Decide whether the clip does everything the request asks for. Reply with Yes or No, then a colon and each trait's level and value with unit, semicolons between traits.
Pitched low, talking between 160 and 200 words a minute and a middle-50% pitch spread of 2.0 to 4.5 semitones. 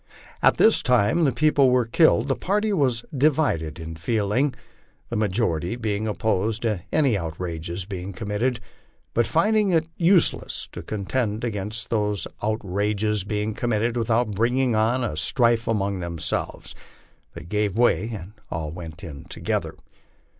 No: low, 110 Hz; average, 145 wpm; average, 4.1 semitones